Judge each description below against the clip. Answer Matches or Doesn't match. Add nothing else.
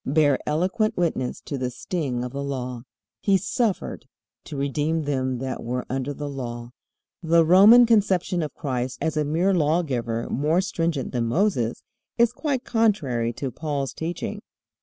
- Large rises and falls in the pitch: Matches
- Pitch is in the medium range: Matches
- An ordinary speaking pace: Matches